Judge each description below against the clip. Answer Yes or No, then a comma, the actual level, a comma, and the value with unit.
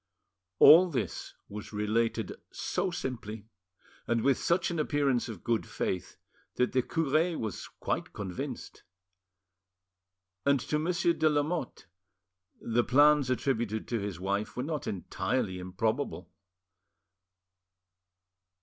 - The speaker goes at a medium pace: No, slow, 115 wpm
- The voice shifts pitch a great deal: Yes, wide, 6.1 semitones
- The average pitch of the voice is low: Yes, low, 125 Hz